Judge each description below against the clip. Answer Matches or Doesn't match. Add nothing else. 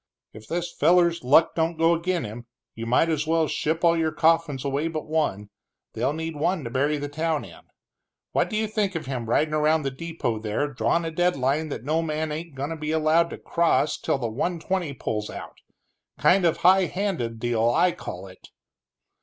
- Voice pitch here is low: Doesn't match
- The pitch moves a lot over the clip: Doesn't match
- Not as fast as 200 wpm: Doesn't match